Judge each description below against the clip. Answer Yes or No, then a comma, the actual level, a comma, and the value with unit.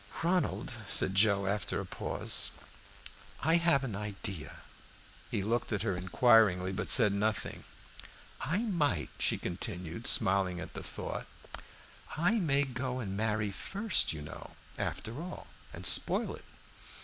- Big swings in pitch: Yes, wide, 6.6 semitones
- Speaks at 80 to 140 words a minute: Yes, slow, 135 wpm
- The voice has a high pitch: No, low, 110 Hz